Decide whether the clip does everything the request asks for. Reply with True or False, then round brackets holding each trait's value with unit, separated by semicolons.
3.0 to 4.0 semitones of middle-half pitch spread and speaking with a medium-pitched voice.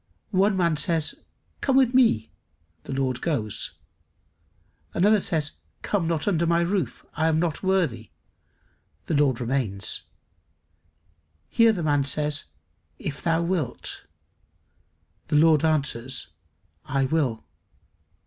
False (4.4 semitones; 155 Hz)